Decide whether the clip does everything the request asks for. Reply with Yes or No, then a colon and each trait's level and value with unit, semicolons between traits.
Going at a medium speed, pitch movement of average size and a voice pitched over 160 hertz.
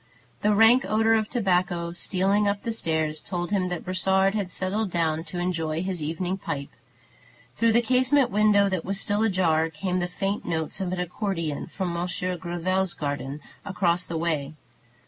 Yes: average, 170 wpm; average, 3.2 semitones; medium, 185 Hz